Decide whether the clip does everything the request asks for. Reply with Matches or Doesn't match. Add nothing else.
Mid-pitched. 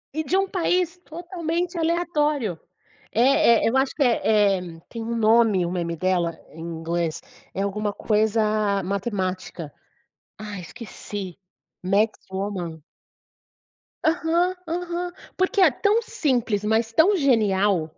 Doesn't match